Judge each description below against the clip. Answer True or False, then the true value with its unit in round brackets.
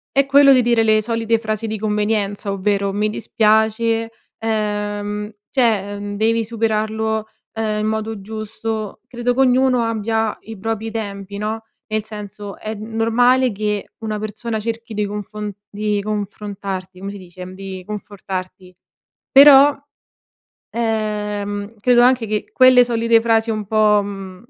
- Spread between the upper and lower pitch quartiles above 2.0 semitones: False (1.7 semitones)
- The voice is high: True (215 Hz)